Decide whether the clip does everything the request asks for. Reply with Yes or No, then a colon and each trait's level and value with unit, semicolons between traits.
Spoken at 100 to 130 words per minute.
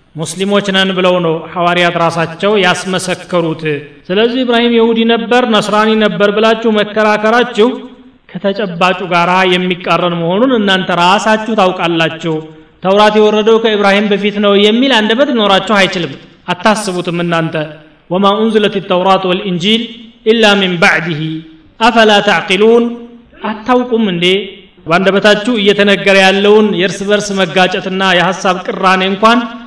Yes: fast, 110 wpm